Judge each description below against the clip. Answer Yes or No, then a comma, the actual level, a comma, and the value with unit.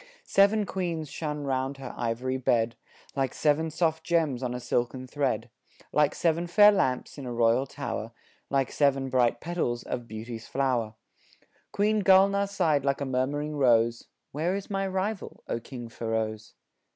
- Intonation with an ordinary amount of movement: No, wide, 5.7 semitones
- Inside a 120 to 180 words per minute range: Yes, average, 155 wpm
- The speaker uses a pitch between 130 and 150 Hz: Yes, low, 135 Hz